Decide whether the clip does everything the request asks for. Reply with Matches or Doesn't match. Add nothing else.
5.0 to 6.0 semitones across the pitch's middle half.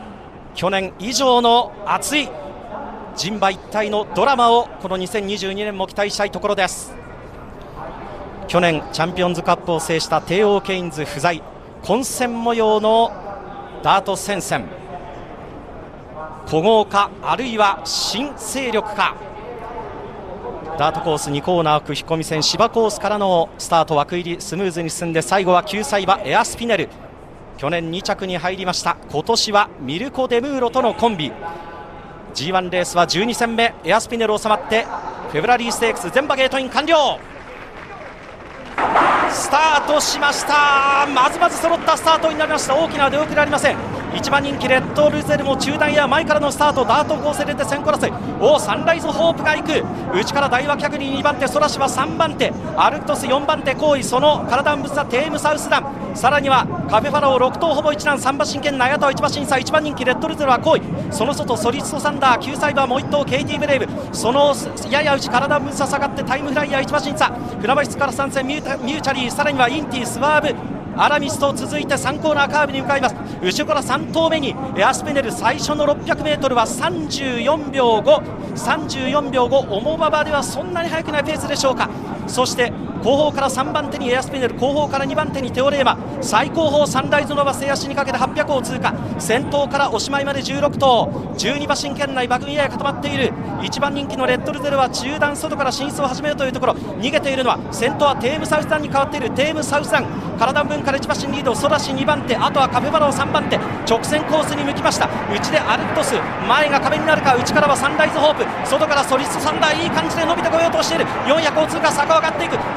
Matches